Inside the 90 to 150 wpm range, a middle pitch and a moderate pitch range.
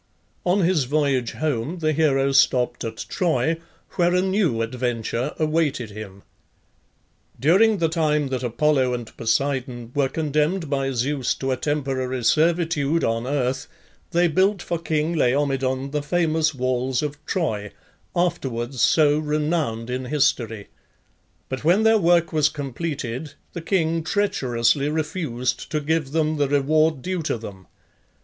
Yes: average, 140 wpm; medium, 145 Hz; average, 4.0 semitones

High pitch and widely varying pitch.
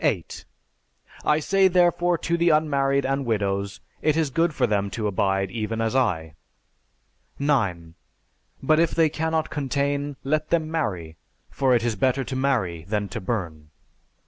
No: low, 135 Hz; wide, 7.4 semitones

